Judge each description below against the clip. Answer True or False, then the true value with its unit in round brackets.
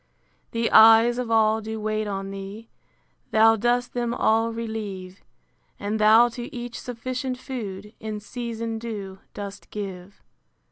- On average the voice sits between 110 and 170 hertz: False (220 Hz)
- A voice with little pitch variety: True (2.2 semitones)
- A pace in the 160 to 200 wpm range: False (135 wpm)